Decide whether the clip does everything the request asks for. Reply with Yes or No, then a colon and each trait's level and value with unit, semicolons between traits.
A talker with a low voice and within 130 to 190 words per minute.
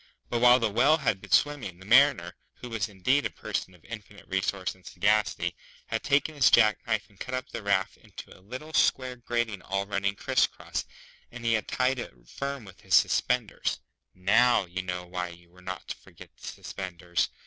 No: low, 105 Hz; average, 200 wpm